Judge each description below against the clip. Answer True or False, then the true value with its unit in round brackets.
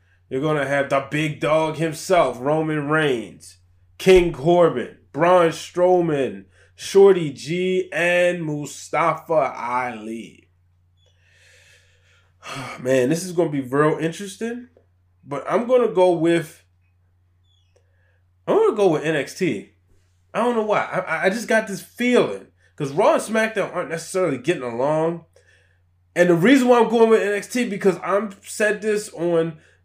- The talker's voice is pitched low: False (155 Hz)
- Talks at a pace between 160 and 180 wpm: False (135 wpm)